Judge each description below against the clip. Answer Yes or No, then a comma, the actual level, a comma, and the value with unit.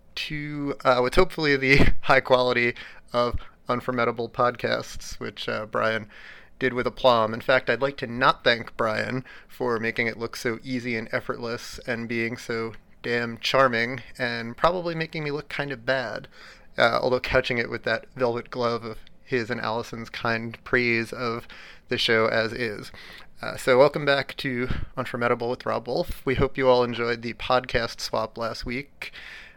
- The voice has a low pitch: Yes, low, 125 Hz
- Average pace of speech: Yes, average, 170 wpm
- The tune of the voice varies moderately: No, narrow, 2.1 semitones